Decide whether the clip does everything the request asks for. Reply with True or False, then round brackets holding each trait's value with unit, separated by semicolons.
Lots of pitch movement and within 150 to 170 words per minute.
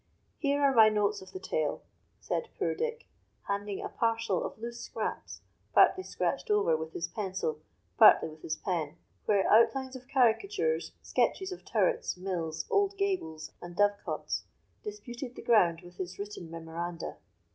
True (8.1 semitones; 155 wpm)